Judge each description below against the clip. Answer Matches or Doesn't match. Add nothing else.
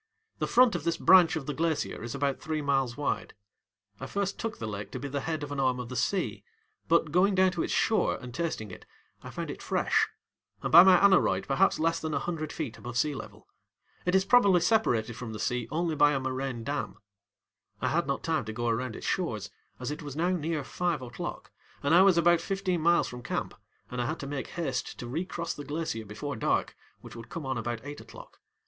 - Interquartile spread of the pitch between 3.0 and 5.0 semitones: Doesn't match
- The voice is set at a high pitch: Doesn't match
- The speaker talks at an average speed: Doesn't match